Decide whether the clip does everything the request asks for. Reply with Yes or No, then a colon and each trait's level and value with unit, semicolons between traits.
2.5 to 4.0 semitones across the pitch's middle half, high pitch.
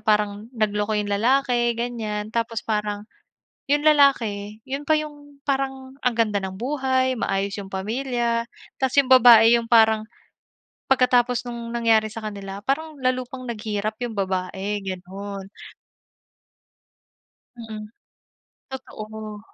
Yes: average, 3.6 semitones; high, 225 Hz